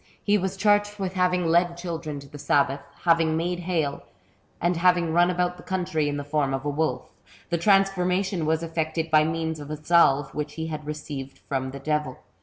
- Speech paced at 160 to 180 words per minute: No, average, 200 wpm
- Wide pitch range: No, average, 3.1 semitones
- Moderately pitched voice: Yes, medium, 160 Hz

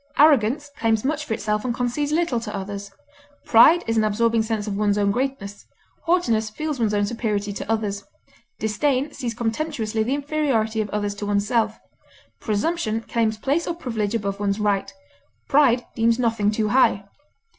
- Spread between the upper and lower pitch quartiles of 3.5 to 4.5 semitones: Yes, average, 3.9 semitones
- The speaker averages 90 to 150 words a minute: No, average, 165 wpm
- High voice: Yes, high, 225 Hz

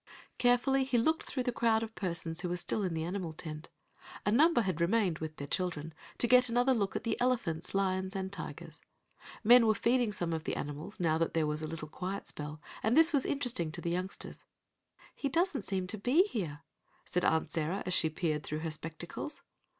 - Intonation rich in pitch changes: Yes, wide, 6.7 semitones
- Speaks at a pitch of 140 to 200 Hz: Yes, high, 190 Hz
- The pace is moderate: No, fast, 210 wpm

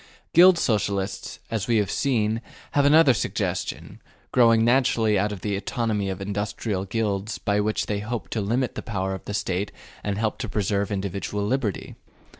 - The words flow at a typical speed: Yes, average, 170 wpm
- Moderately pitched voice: No, low, 105 Hz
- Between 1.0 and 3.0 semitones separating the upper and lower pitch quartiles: Yes, narrow, 2.6 semitones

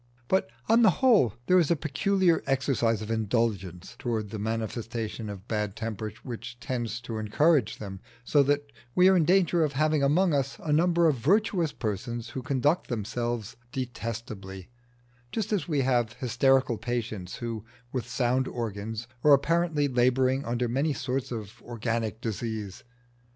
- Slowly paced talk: No, average, 155 wpm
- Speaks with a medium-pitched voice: No, low, 120 Hz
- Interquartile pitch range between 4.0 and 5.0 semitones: Yes, average, 4.6 semitones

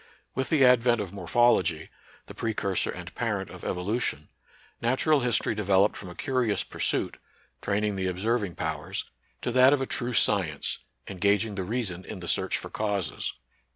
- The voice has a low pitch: Yes, low, 105 Hz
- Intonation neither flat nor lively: Yes, average, 4.5 semitones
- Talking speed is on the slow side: No, average, 165 wpm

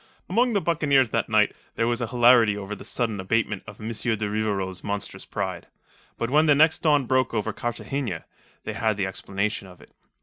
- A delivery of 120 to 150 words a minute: No, average, 190 wpm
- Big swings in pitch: No, average, 4.2 semitones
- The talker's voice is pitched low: Yes, low, 115 Hz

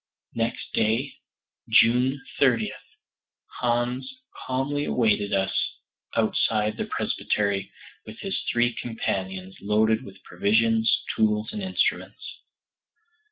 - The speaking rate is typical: No, slow, 95 wpm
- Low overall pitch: Yes, low, 115 Hz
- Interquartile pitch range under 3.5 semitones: Yes, average, 2.7 semitones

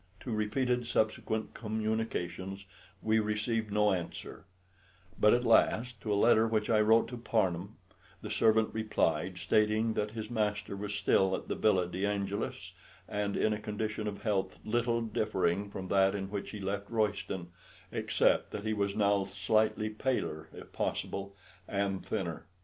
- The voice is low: Yes, low, 105 Hz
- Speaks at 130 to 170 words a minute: Yes, average, 155 wpm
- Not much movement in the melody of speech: Yes, narrow, 1.9 semitones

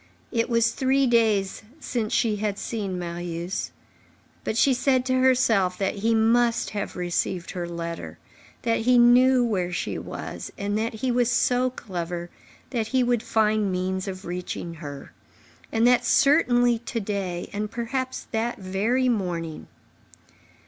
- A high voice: Yes, high, 220 Hz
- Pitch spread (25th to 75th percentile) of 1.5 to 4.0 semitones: No, average, 4.7 semitones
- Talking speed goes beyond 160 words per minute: No, average, 145 wpm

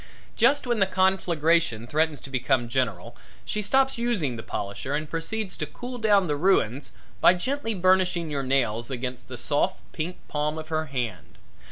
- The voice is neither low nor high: Yes, medium, 155 Hz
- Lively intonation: Yes, wide, 6.5 semitones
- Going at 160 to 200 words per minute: Yes, average, 170 wpm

